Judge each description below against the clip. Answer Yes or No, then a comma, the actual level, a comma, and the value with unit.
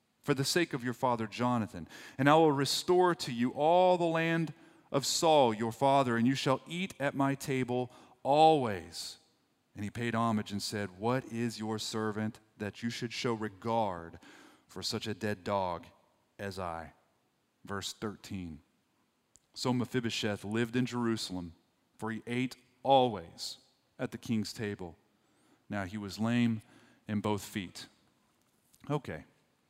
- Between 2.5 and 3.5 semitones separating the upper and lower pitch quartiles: No, average, 4.0 semitones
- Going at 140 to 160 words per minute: Yes, average, 145 wpm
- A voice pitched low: Yes, low, 115 Hz